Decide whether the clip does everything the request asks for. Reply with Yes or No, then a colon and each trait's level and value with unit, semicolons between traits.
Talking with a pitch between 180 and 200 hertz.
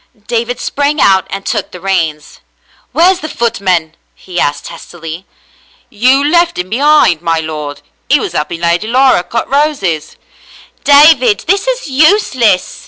No: high, 225 Hz